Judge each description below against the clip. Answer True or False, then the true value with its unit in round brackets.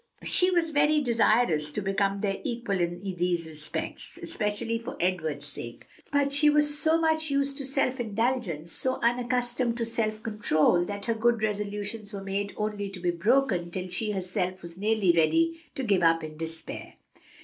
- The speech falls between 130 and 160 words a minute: False (170 wpm)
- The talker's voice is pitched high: True (210 Hz)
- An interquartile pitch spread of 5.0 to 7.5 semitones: True (5.5 semitones)